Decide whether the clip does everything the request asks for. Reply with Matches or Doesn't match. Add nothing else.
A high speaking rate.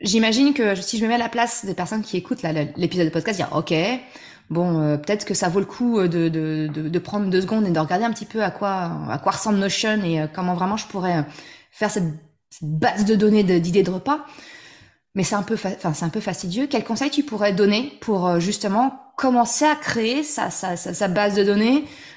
Matches